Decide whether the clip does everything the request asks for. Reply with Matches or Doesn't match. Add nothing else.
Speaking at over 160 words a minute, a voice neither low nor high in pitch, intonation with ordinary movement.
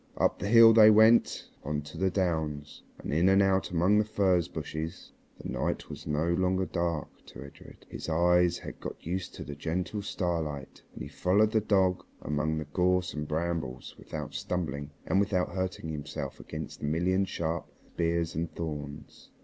Doesn't match